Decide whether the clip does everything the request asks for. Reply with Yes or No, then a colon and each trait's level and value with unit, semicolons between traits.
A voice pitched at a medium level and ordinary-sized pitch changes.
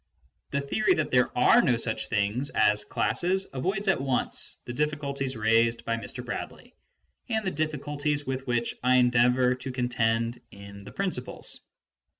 No: low, 125 Hz; average, 3.9 semitones